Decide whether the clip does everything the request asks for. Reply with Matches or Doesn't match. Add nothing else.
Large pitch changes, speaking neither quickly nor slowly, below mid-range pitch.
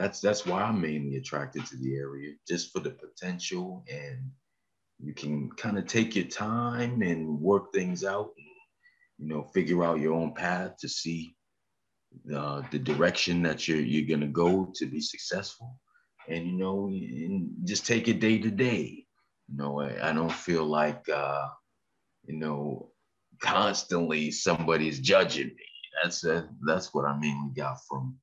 Matches